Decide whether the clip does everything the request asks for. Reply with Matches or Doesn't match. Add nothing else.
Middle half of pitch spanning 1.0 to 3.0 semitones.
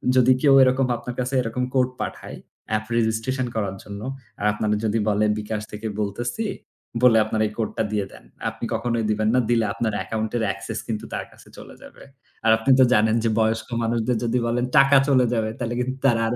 Matches